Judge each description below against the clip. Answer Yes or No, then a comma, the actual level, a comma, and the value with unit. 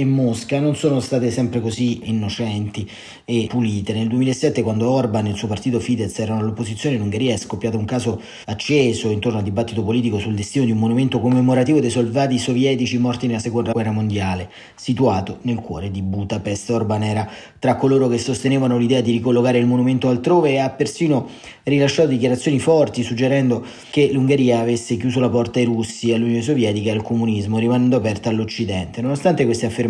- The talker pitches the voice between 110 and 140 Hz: Yes, low, 120 Hz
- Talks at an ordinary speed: No, fast, 180 wpm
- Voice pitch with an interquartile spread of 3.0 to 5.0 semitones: No, narrow, 2.6 semitones